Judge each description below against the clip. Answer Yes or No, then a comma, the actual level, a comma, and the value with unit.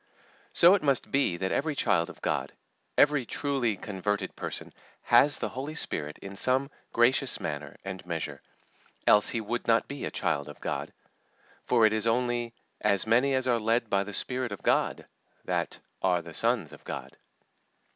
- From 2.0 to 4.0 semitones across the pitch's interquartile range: No, average, 5.2 semitones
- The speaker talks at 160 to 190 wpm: Yes, average, 175 wpm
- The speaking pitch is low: Yes, low, 115 Hz